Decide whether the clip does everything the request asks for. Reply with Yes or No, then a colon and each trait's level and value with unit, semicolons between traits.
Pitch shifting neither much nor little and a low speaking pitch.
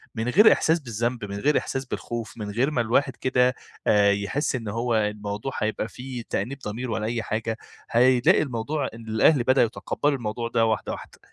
Yes: average, 3.1 semitones; low, 120 Hz